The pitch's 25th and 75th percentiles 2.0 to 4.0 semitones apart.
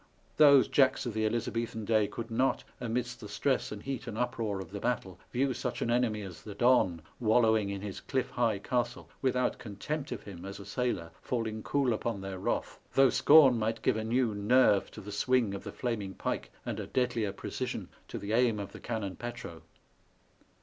Yes: average, 3.4 semitones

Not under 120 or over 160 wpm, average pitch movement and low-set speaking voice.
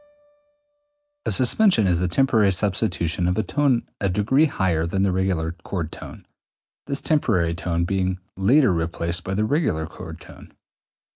Yes: average, 150 wpm; average, 4.8 semitones; very low, 95 Hz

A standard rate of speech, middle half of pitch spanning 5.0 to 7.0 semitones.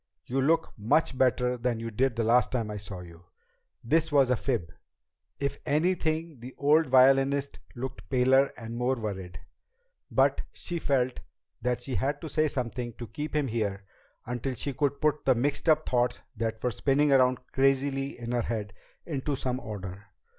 No: average, 175 wpm; average, 3.3 semitones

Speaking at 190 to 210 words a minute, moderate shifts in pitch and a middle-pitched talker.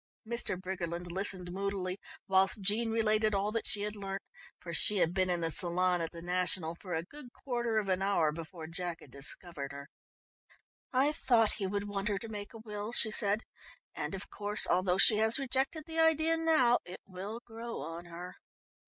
No: average, 195 wpm; average, 3.9 semitones; high, 195 Hz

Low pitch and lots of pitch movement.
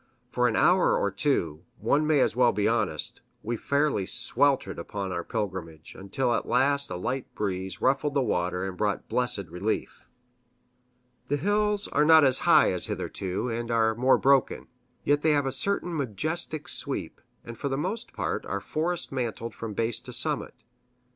Yes: low, 125 Hz; wide, 6.0 semitones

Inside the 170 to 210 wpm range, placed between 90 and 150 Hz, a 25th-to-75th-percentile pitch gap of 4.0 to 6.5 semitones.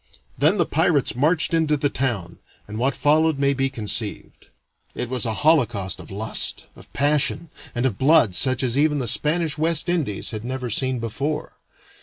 Yes: average, 175 wpm; low, 135 Hz; average, 4.6 semitones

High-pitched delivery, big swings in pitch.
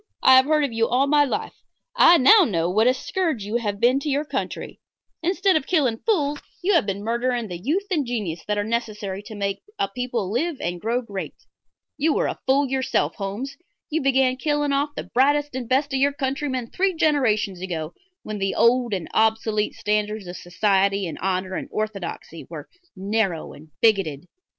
Yes: high, 235 Hz; wide, 5.9 semitones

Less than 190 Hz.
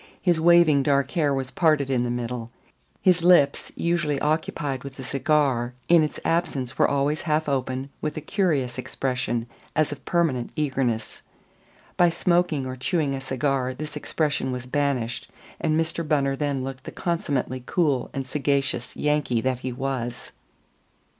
Yes: medium, 140 Hz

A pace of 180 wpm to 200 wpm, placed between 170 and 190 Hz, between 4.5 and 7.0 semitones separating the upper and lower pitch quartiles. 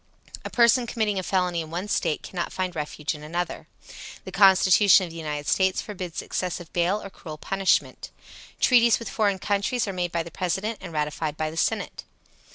No: average, 185 wpm; medium, 185 Hz; average, 3.4 semitones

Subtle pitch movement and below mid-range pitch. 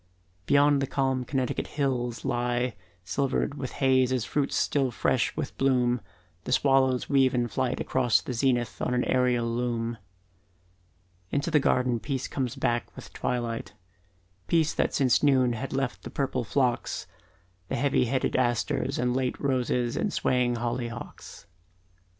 Yes: narrow, 1.9 semitones; low, 125 Hz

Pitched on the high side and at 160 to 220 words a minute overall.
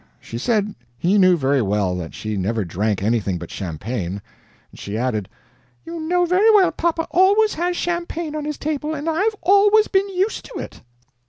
Yes: very high, 285 Hz; average, 175 wpm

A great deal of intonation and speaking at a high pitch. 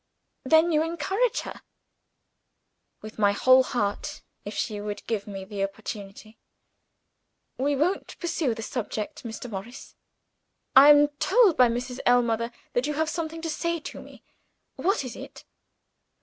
Yes: wide, 6.6 semitones; very high, 250 Hz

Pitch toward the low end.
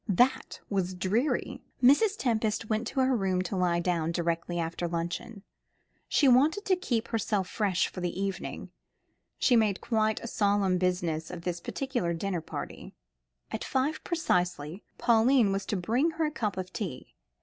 No: high, 200 Hz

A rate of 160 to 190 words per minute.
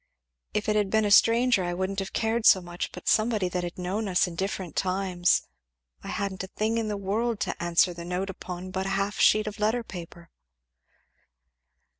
No: average, 200 wpm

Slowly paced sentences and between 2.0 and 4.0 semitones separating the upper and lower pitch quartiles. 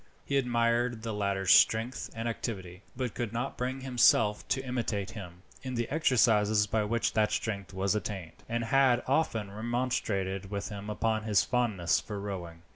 No: average, 165 wpm; average, 3.4 semitones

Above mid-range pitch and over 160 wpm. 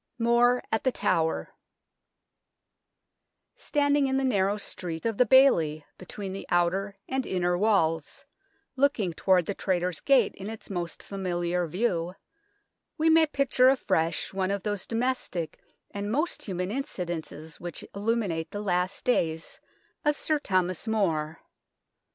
No: high, 195 Hz; slow, 135 wpm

